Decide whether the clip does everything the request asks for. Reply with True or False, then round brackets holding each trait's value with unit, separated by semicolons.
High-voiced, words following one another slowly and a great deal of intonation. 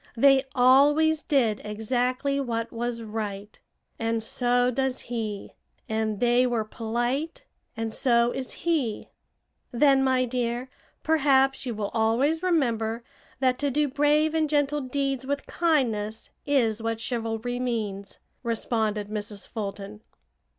False (245 Hz; 125 wpm; 3.5 semitones)